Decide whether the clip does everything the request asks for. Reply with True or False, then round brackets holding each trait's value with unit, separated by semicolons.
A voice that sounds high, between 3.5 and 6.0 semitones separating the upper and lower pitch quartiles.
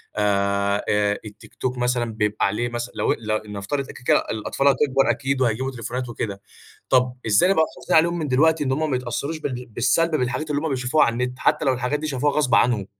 False (125 Hz; 4.3 semitones)